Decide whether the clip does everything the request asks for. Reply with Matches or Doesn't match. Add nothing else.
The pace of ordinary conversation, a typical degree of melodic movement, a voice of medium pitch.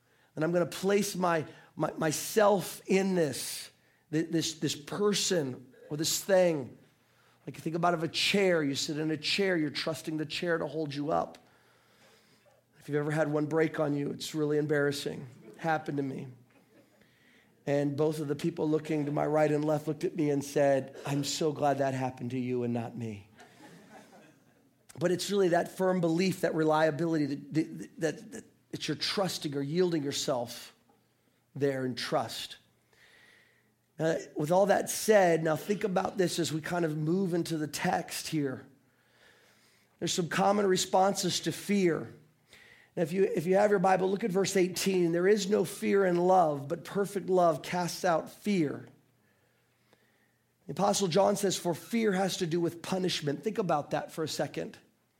Matches